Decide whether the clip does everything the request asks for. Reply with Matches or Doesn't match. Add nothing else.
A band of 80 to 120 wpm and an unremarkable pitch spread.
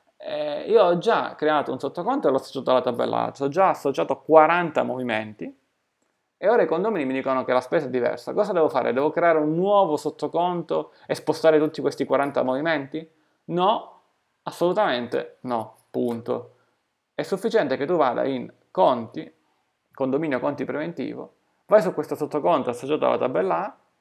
Doesn't match